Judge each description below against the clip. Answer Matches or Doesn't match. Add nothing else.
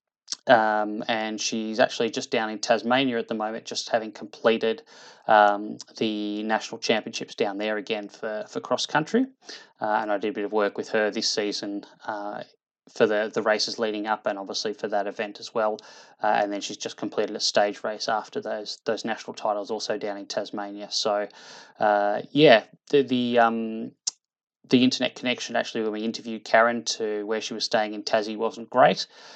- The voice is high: Doesn't match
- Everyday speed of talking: Matches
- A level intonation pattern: Matches